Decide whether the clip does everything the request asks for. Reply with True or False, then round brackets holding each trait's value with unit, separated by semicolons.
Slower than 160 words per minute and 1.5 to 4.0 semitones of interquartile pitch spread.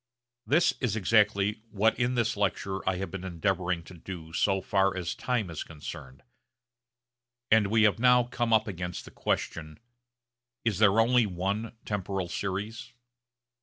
True (150 wpm; 3.6 semitones)